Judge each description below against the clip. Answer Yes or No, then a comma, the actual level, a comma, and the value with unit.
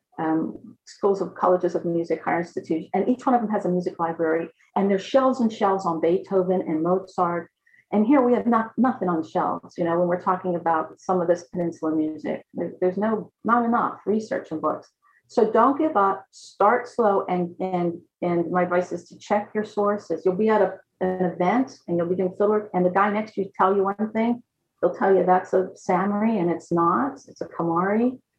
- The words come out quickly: Yes, fast, 215 wpm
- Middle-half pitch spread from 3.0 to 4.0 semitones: Yes, average, 3.6 semitones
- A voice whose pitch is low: No, medium, 185 Hz